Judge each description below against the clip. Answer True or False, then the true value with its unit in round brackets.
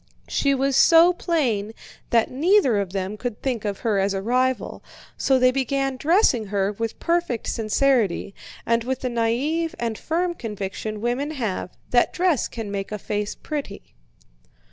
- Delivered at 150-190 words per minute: True (160 wpm)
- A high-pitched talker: True (240 Hz)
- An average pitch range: True (4.8 semitones)